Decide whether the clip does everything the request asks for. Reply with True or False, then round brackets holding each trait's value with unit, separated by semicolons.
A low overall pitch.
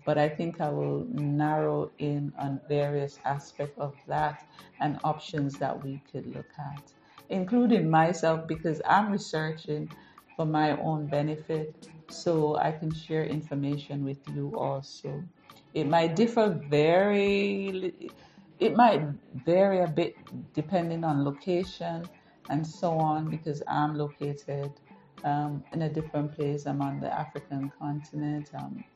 False (150 Hz)